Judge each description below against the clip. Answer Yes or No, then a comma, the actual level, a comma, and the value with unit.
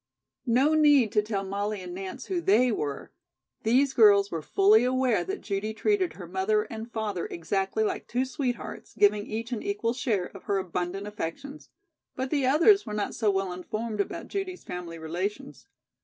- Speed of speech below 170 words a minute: No, average, 175 wpm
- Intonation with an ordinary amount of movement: Yes, average, 4.8 semitones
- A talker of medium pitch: No, high, 215 Hz